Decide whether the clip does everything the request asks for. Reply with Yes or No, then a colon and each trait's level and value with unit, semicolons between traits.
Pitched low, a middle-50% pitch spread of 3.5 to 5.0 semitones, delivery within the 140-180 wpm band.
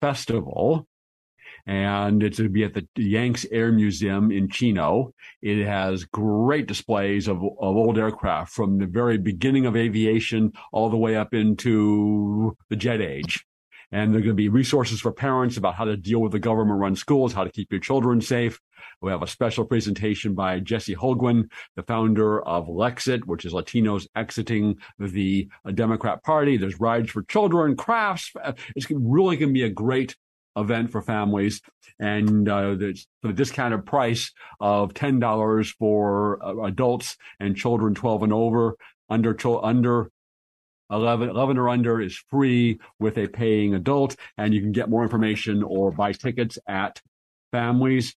No: low, 110 Hz; average, 2.7 semitones; average, 160 wpm